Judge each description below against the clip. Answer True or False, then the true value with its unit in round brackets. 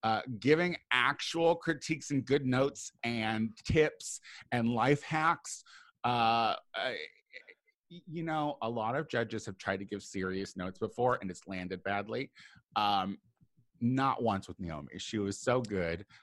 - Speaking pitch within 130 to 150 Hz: False (120 Hz)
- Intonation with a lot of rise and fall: True (7.4 semitones)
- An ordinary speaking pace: True (150 wpm)